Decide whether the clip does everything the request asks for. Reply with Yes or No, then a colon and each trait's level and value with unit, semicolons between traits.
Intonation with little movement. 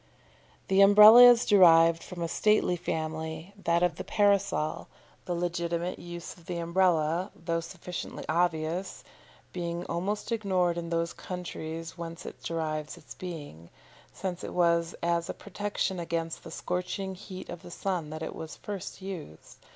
Yes: narrow, 2.1 semitones